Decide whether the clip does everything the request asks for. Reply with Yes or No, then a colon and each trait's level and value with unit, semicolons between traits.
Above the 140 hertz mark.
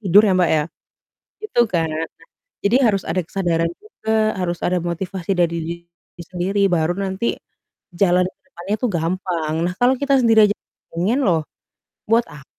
Yes: medium, 185 Hz